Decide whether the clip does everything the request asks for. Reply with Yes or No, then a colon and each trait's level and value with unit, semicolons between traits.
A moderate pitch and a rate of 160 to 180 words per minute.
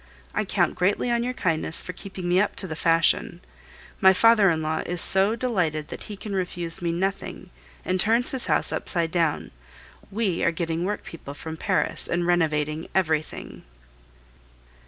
Yes: medium, 175 Hz; average, 165 wpm